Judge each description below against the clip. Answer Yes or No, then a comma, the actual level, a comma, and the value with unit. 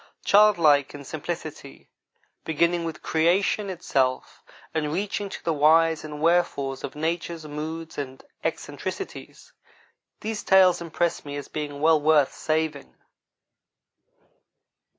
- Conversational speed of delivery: No, slow, 110 wpm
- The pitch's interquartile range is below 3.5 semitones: Yes, average, 2.7 semitones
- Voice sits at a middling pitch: Yes, medium, 160 Hz